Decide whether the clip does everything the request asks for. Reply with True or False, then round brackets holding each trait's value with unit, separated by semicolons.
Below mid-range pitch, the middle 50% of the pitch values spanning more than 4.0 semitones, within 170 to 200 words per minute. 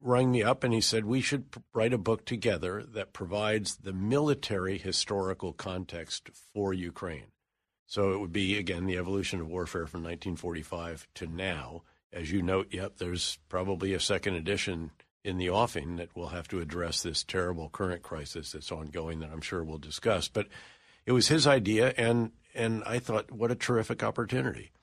True (95 Hz; 4.4 semitones; 180 wpm)